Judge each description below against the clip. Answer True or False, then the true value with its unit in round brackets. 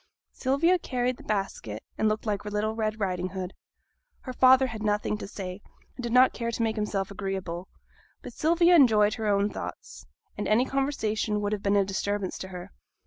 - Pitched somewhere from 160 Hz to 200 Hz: False (215 Hz)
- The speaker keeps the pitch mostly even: False (3.7 semitones)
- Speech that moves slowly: False (190 wpm)